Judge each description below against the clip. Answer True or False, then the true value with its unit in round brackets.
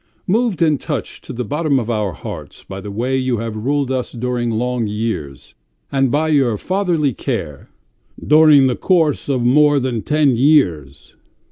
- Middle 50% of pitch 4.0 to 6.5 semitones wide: True (4.6 semitones)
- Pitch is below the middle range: True (130 Hz)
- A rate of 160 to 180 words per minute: True (170 wpm)